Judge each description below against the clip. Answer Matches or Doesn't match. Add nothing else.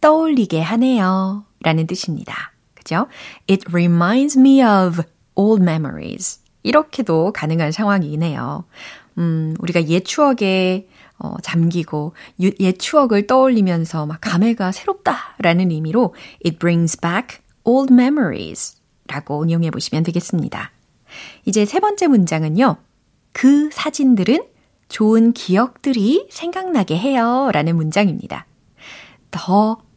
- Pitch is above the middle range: Matches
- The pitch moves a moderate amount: Doesn't match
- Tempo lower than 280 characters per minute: Doesn't match